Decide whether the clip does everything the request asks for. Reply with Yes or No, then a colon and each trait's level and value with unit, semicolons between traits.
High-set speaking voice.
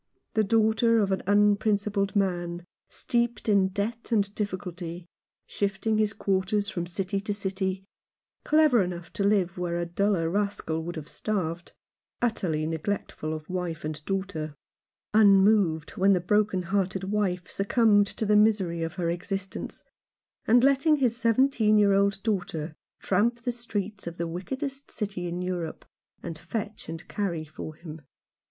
Yes: high, 195 Hz